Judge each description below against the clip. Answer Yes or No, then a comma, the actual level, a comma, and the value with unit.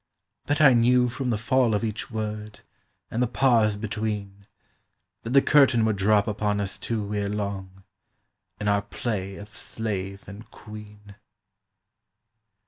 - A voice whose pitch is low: Yes, low, 105 Hz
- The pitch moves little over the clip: Yes, narrow, 2.3 semitones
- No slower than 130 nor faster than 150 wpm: Yes, average, 140 wpm